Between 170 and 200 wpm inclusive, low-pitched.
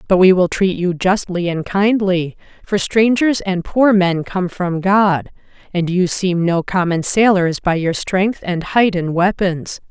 No: average, 175 wpm; medium, 185 Hz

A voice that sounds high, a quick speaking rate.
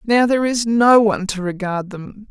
Yes: high, 210 Hz; fast, 210 wpm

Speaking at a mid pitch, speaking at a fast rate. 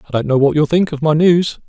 Yes: medium, 155 Hz; fast, 320 wpm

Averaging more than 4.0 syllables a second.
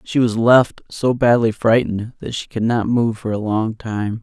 Yes: 4.5 syllables/s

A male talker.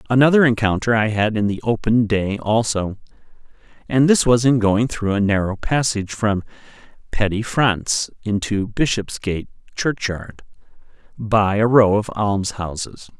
Yes: male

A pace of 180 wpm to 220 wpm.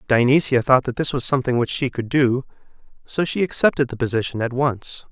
Yes: average, 200 wpm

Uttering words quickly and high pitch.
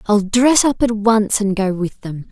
Yes: fast, 235 wpm; high, 215 Hz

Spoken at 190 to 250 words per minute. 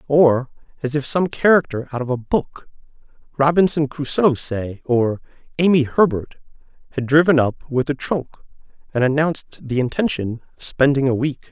No: average, 150 wpm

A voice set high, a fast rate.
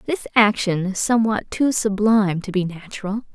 No: high, 205 Hz; average, 160 wpm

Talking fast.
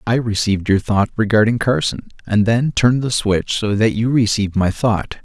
No: average, 195 wpm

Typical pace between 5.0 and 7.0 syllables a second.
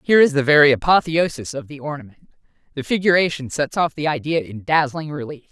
Yes: 6.0 syllables/s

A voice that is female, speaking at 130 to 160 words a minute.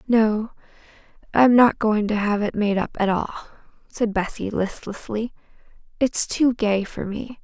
Yes: female; average, 155 wpm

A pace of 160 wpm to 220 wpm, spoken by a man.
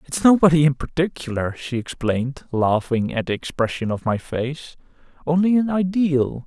No: average, 150 wpm; male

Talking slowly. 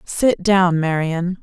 Yes: slow, 125 wpm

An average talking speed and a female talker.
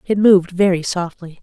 Yes: average, 170 wpm; female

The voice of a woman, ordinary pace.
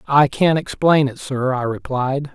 No: male; average, 180 wpm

